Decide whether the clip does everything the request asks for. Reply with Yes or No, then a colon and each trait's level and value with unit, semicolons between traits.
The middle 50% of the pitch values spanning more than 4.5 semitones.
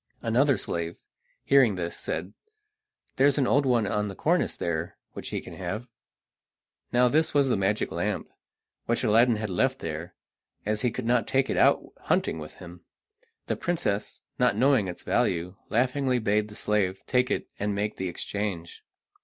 Yes: average, 5.2 semitones